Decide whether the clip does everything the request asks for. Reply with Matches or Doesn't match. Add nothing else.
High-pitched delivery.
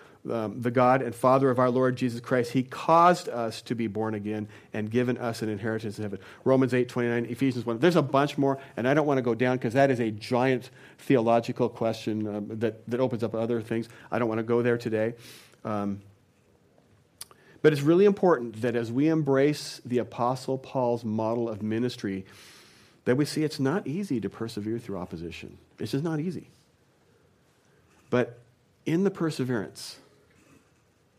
Doesn't match